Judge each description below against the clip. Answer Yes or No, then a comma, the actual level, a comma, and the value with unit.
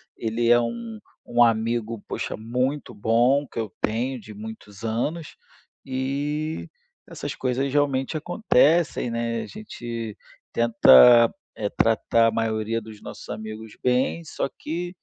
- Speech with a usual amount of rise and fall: Yes, average, 3.8 semitones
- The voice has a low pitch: Yes, low, 120 Hz